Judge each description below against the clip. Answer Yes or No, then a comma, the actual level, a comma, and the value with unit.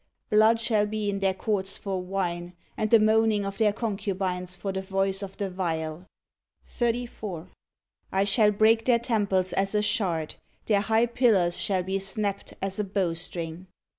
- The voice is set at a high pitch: Yes, high, 195 Hz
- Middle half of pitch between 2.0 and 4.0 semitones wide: Yes, narrow, 2.6 semitones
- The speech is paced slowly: No, average, 165 wpm